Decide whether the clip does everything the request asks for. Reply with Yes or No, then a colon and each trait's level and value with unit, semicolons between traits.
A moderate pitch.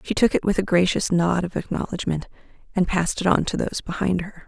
Yes: medium, 180 Hz